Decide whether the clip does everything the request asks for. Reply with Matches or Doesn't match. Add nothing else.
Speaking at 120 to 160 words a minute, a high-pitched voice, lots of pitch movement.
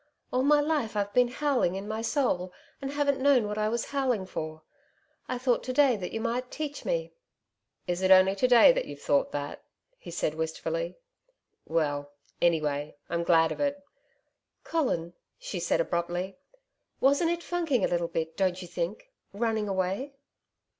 Doesn't match